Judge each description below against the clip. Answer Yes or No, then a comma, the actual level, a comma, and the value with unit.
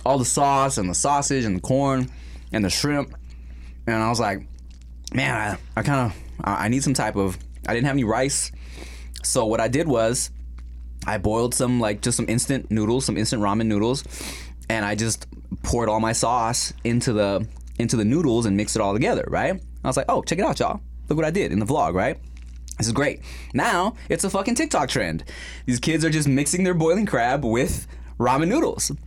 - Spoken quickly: Yes, fast, 215 wpm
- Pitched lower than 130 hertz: Yes, low, 110 Hz